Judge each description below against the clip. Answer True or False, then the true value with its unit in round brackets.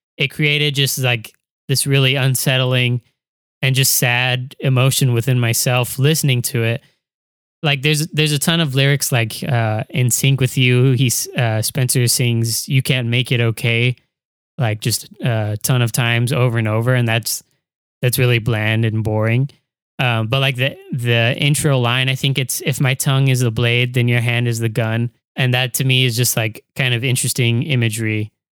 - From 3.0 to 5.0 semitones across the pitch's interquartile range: False (2.4 semitones)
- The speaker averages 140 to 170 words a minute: False (185 wpm)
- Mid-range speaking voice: False (125 Hz)